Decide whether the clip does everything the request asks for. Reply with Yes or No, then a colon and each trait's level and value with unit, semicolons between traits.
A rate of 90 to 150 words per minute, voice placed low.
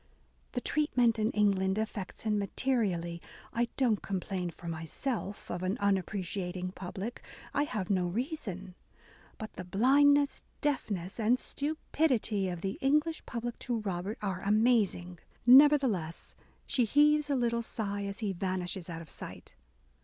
No: average, 140 wpm; high, 210 Hz